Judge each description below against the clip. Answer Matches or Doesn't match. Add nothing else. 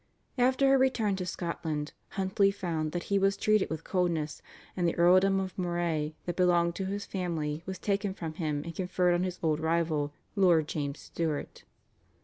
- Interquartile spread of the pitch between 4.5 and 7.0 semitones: Doesn't match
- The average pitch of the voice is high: Doesn't match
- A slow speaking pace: Doesn't match